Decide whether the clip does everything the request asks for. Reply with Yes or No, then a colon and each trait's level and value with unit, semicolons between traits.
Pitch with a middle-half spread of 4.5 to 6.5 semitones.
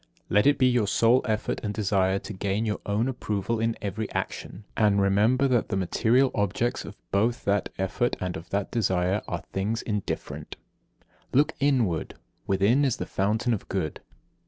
No: average, 3.4 semitones